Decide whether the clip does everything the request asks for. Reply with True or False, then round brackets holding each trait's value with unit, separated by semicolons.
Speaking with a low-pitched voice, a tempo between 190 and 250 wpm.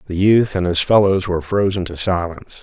True (95 Hz; 205 wpm)